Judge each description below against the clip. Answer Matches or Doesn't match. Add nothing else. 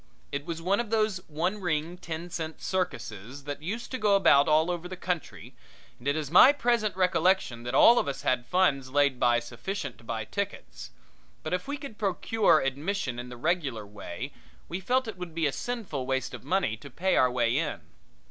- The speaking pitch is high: Doesn't match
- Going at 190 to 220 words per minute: Matches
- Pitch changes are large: Matches